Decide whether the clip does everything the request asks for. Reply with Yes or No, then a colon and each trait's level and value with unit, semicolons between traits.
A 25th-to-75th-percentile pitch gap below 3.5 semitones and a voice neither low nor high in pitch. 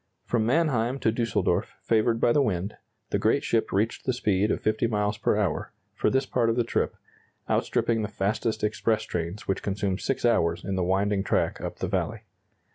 No: average, 2.8 semitones; low, 110 Hz